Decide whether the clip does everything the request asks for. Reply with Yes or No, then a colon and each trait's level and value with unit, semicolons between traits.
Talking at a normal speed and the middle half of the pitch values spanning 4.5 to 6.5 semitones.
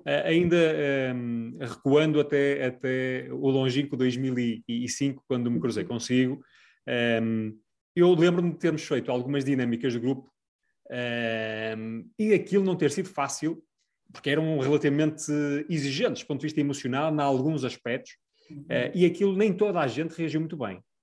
No: average, 145 wpm; average, 4.0 semitones